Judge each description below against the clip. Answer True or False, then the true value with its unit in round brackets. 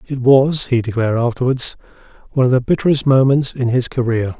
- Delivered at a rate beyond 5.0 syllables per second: True (6.0 syllables/s)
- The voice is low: True (125 Hz)